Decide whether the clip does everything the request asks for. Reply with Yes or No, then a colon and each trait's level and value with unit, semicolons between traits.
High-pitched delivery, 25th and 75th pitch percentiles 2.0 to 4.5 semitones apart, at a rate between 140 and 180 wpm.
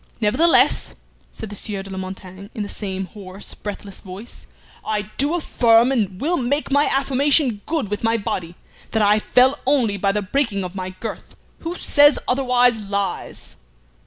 No: high, 215 Hz; average, 5.2 semitones; average, 165 wpm